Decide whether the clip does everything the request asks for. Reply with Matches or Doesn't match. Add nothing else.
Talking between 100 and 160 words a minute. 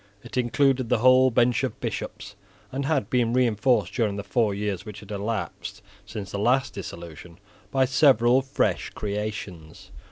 Matches